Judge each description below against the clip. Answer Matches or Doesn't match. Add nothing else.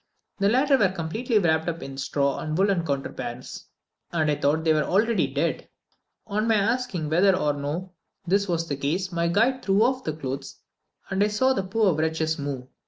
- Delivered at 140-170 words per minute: Doesn't match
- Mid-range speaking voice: Matches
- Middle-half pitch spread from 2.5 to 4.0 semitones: Doesn't match